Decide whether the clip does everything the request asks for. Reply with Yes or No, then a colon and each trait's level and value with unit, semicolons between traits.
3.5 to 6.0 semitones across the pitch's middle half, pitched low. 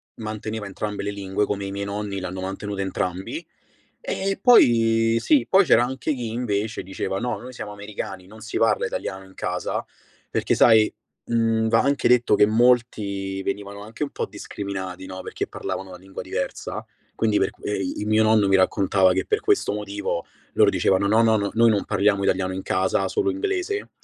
No: average, 2.8 semitones; low, 105 Hz